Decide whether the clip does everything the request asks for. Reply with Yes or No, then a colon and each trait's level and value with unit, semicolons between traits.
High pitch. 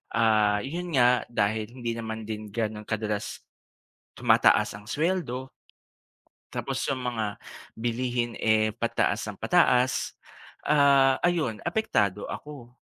No: low, 115 Hz